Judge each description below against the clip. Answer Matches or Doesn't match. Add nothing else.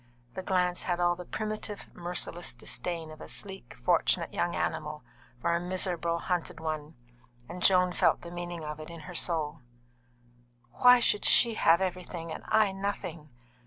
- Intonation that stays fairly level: Matches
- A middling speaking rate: Matches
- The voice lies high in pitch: Doesn't match